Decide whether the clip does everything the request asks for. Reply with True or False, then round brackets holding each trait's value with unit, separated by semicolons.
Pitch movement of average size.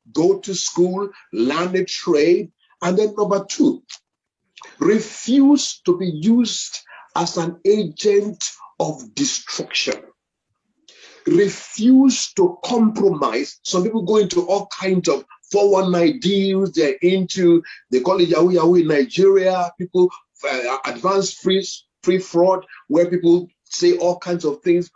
True (3.5 semitones)